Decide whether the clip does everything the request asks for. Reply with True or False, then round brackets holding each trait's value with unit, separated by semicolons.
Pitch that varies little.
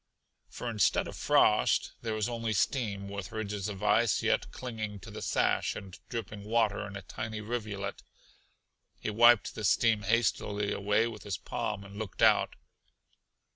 True (2.2 semitones)